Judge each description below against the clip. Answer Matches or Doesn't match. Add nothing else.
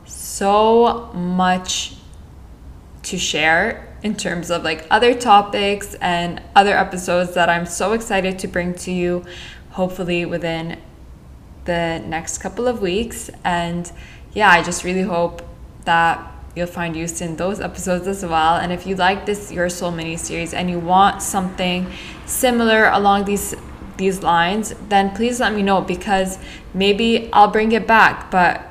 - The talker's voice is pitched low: Doesn't match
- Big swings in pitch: Doesn't match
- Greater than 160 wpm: Doesn't match